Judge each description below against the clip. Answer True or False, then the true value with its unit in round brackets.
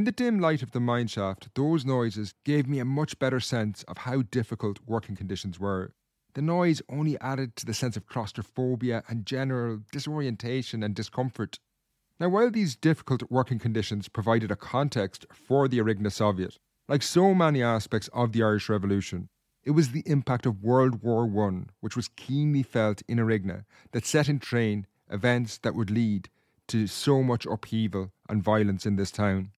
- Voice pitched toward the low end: True (115 Hz)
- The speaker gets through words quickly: False (180 wpm)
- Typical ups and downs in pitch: True (4.1 semitones)